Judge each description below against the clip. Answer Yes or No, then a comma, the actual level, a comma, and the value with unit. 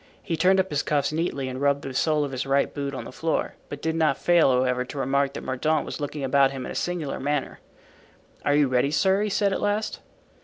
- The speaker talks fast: Yes, fast, 240 wpm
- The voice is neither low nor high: Yes, medium, 145 Hz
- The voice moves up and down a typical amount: Yes, average, 3.1 semitones